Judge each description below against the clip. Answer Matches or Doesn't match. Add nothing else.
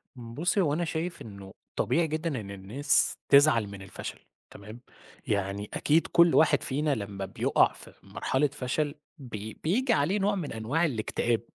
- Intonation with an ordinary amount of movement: Doesn't match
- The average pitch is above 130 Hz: Matches